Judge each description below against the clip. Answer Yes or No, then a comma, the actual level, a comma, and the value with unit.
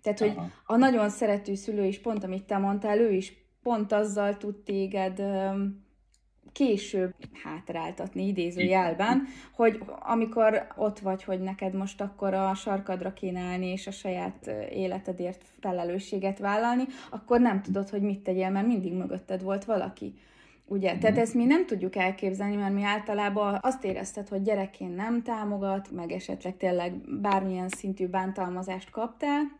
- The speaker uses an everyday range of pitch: No, narrow, 2.1 semitones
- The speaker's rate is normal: Yes, average, 145 wpm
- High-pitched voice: Yes, high, 200 Hz